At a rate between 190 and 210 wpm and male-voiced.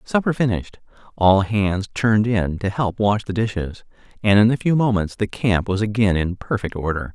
Yes: average, 195 wpm; male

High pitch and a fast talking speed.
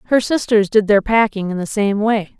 Yes: high, 210 Hz; fast, 225 wpm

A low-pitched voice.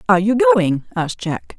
No: high, 220 Hz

